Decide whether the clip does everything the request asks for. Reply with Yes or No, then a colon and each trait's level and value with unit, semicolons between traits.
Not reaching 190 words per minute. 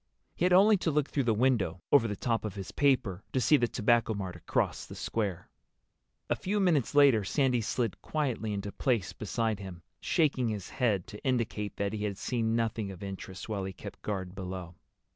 No: average, 200 wpm